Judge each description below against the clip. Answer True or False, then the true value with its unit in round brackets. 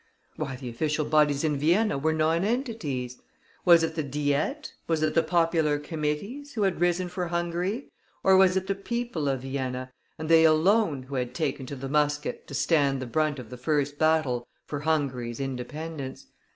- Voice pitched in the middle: True (155 Hz)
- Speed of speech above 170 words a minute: True (180 wpm)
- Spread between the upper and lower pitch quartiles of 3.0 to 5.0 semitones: True (3.9 semitones)